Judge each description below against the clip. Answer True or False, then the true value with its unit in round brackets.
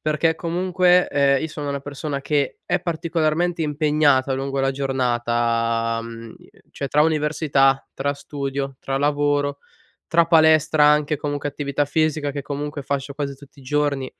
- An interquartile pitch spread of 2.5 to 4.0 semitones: False (2.1 semitones)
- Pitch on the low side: False (145 Hz)